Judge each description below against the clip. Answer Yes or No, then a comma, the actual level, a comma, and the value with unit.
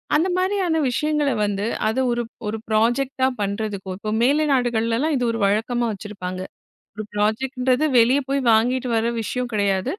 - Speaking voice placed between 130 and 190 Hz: No, high, 235 Hz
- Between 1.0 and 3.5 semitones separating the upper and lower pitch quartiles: No, average, 3.9 semitones